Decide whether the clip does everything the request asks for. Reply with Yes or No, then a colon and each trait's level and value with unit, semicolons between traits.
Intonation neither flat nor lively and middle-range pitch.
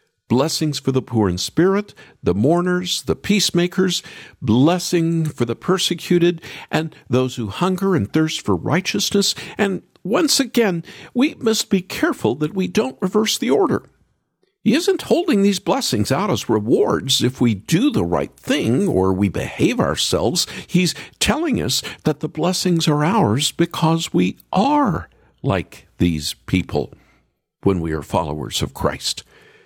No: wide, 7.2 semitones; medium, 170 Hz